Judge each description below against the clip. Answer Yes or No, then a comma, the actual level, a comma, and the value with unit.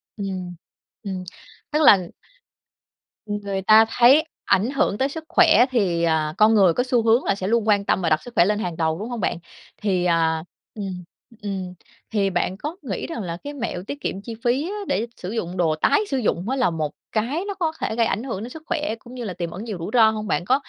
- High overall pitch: Yes, high, 210 Hz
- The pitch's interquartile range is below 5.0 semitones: No, average, 5.3 semitones